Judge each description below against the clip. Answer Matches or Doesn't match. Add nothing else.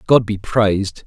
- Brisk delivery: Doesn't match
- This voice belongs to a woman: Doesn't match